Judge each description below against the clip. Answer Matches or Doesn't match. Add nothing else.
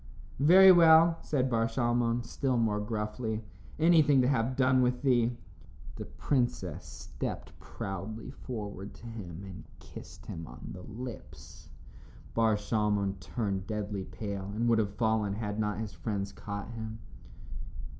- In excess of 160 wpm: Doesn't match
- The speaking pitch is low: Matches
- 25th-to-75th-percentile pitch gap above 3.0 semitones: Matches